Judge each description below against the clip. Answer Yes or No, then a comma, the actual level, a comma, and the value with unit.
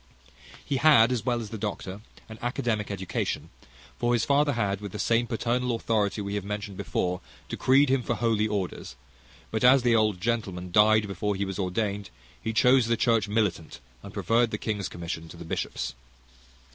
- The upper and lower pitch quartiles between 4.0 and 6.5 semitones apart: No, average, 2.9 semitones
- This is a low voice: Yes, low, 110 Hz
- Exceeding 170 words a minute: Yes, average, 185 wpm